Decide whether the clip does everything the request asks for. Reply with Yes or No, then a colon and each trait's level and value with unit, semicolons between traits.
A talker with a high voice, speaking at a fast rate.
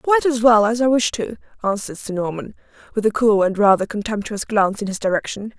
Yes: high, 215 Hz; fast, 215 wpm